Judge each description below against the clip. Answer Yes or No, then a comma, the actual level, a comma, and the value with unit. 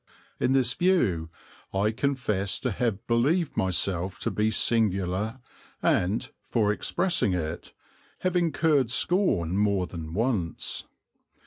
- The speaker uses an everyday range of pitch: No, wide, 6.0 semitones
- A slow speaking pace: Yes, slow, 115 wpm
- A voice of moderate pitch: No, low, 105 Hz